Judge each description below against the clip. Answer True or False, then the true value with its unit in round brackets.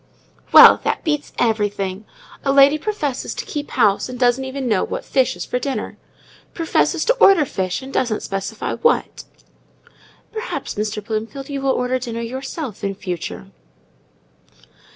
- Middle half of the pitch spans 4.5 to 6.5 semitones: True (4.8 semitones)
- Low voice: False (250 Hz)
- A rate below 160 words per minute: True (150 wpm)